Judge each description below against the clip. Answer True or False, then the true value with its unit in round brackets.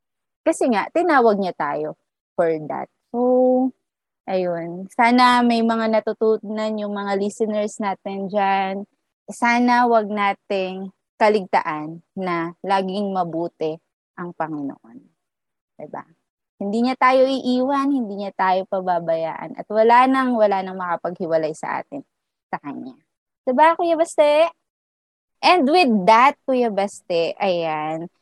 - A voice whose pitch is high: True (205 Hz)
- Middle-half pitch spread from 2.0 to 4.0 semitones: False (5.2 semitones)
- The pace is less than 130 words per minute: True (115 wpm)